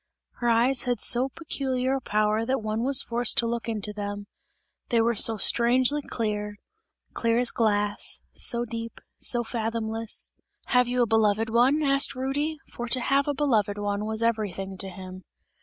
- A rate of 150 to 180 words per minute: Yes, average, 170 wpm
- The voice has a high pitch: Yes, high, 230 Hz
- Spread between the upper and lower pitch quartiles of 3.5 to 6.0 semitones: No, average, 3.0 semitones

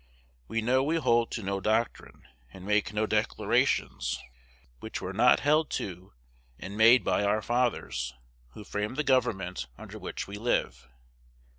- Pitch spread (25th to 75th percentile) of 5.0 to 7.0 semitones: No, average, 3.9 semitones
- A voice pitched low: Yes, low, 110 Hz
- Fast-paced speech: No, average, 150 wpm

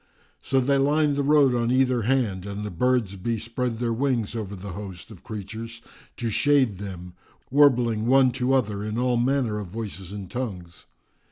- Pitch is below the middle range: Yes, low, 115 Hz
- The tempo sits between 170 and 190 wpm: Yes, average, 175 wpm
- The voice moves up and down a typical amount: Yes, average, 4.1 semitones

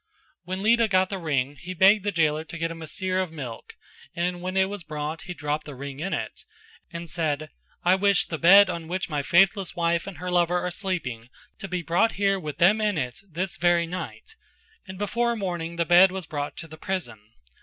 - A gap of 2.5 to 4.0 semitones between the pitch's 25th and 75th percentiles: Yes, average, 3.2 semitones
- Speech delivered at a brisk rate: Yes, fast, 220 wpm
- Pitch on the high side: No, medium, 175 Hz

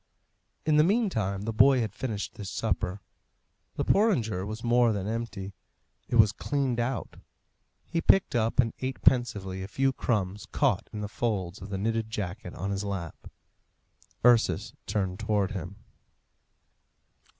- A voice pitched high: No, low, 110 Hz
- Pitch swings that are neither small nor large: Yes, average, 3.7 semitones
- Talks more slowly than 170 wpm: Yes, average, 150 wpm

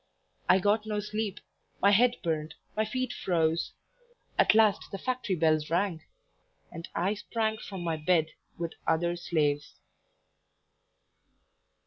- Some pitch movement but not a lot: Yes, average, 4.5 semitones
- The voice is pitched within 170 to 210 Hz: Yes, medium, 185 Hz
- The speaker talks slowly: Yes, slow, 125 wpm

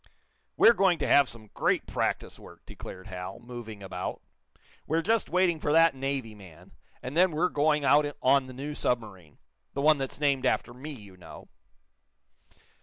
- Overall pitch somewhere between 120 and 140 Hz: Yes, low, 135 Hz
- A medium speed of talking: Yes, average, 170 wpm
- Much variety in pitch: Yes, wide, 5.8 semitones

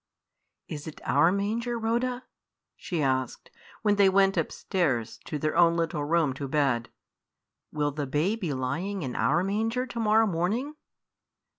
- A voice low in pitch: No, medium, 170 Hz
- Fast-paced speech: No, average, 150 wpm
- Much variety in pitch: Yes, wide, 6.4 semitones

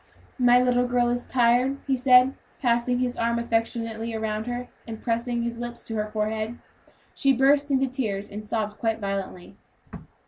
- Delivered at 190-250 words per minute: No, average, 165 wpm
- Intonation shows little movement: Yes, narrow, 2.0 semitones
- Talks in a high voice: Yes, high, 235 Hz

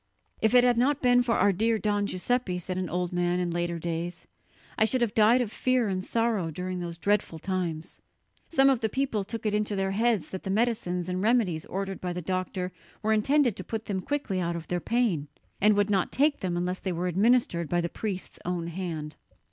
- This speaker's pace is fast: Yes, fast, 220 wpm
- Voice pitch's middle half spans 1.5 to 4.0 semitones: No, average, 4.4 semitones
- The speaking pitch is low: No, high, 195 Hz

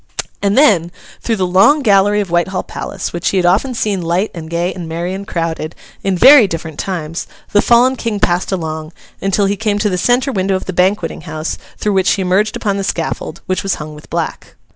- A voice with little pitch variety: No, average, 3.2 semitones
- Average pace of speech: No, fast, 215 wpm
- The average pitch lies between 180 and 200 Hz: Yes, high, 190 Hz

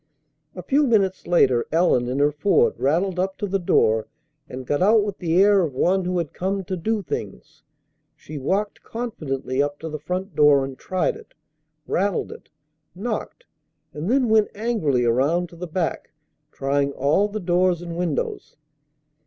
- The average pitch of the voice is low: No, medium, 175 Hz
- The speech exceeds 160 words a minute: Yes, average, 170 wpm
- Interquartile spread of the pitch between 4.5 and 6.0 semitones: Yes, wide, 5.5 semitones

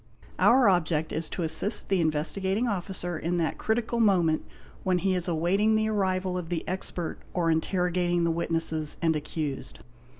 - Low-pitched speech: No, medium, 175 Hz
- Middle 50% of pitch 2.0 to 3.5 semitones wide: Yes, average, 2.9 semitones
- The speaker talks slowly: No, average, 160 wpm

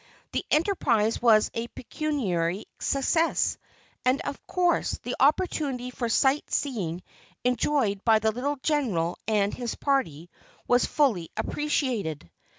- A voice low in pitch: No, high, 245 Hz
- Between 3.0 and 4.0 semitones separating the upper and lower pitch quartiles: No, wide, 5.6 semitones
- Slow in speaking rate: Yes, slow, 120 wpm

